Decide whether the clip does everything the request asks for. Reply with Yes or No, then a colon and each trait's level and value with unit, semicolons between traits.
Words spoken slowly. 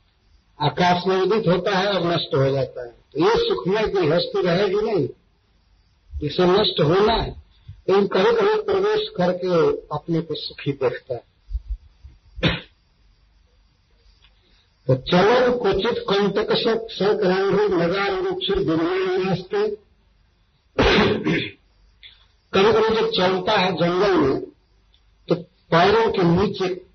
No: average, 120 wpm